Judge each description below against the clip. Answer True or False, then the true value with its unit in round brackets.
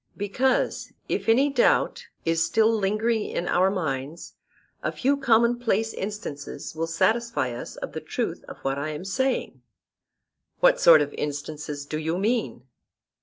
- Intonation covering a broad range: True (7.2 semitones)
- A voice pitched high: True (195 Hz)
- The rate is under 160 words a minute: True (145 wpm)